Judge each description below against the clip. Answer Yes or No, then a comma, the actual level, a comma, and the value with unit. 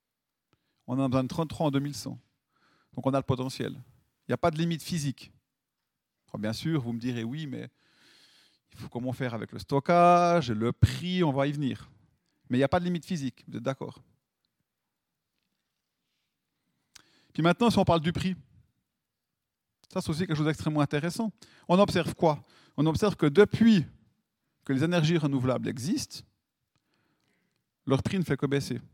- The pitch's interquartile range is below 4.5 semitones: No, average, 4.9 semitones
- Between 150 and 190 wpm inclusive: Yes, average, 175 wpm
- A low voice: No, medium, 145 Hz